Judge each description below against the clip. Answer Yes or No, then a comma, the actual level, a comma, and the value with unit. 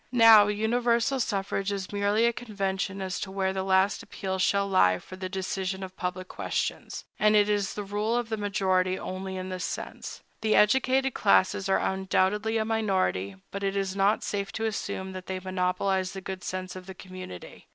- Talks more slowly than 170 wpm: No, average, 190 wpm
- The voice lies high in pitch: Yes, high, 195 Hz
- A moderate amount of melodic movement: No, narrow, 1.9 semitones